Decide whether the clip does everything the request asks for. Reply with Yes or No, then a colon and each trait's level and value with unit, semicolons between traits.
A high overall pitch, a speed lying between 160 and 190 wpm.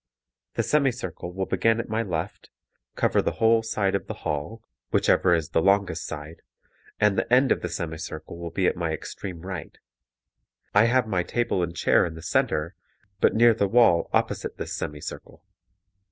No: very low, 95 Hz; average, 185 wpm